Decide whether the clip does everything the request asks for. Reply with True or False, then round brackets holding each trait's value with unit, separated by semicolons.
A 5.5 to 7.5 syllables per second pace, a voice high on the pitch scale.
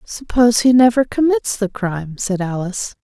False (5.2 syllables/s; 220 Hz)